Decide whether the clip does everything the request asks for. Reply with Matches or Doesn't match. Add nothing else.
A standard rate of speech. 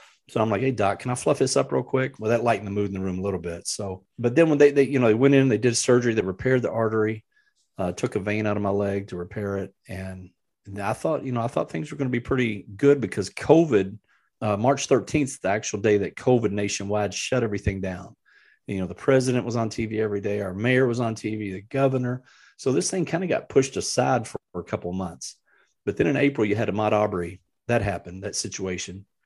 Doesn't match